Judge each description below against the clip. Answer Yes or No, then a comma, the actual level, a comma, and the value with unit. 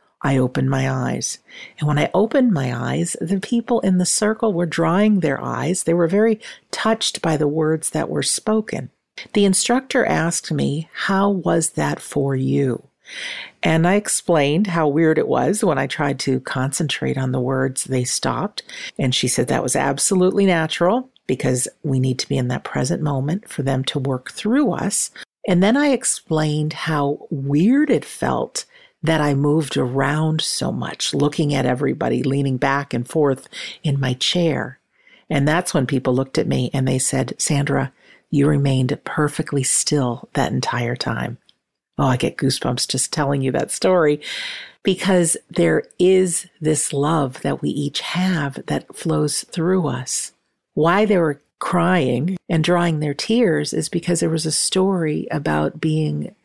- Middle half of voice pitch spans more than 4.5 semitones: Yes, average, 4.9 semitones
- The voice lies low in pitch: No, medium, 155 Hz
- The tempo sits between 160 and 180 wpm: Yes, average, 165 wpm